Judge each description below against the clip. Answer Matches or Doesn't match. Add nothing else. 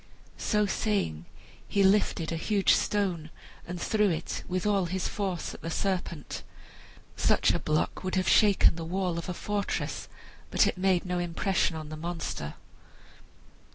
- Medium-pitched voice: Matches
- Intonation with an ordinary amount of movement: Matches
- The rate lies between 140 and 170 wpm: Matches